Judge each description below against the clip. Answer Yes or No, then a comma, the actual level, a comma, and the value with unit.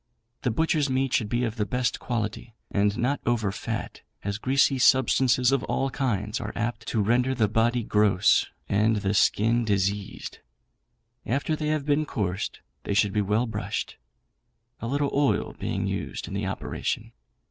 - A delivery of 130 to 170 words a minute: Yes, average, 165 wpm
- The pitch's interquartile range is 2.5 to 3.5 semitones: No, average, 4.0 semitones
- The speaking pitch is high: No, low, 115 Hz